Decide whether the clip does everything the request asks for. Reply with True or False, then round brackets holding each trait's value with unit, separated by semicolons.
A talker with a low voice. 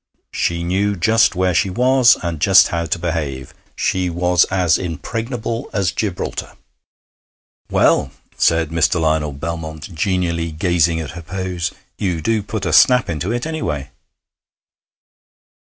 True (90 Hz)